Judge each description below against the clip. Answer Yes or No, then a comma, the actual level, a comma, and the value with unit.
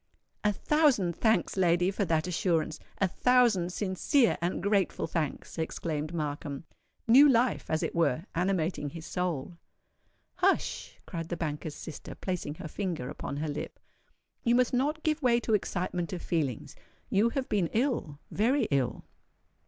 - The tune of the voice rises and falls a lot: Yes, wide, 6.1 semitones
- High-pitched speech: No, medium, 180 Hz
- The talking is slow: No, average, 145 wpm